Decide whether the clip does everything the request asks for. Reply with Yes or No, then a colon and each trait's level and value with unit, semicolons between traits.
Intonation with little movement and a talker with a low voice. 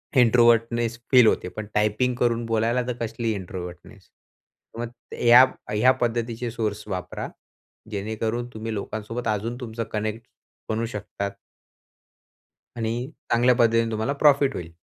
Yes: narrow, 1.9 semitones; low, 115 Hz